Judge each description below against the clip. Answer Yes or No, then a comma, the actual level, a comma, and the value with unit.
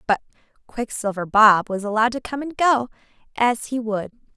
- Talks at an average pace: Yes, average, 165 wpm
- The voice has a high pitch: Yes, high, 225 Hz